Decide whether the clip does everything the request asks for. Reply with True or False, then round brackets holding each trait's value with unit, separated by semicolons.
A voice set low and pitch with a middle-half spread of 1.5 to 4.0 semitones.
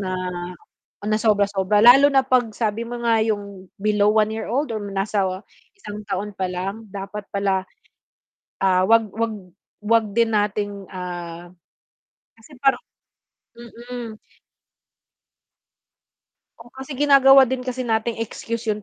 False (215 Hz; 2.9 semitones)